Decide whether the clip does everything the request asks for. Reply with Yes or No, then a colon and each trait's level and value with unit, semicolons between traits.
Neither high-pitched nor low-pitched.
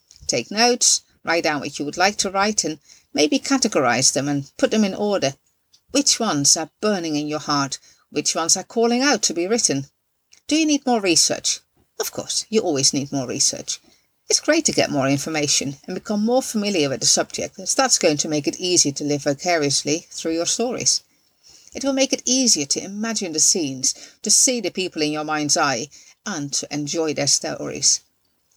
Yes: medium, 165 Hz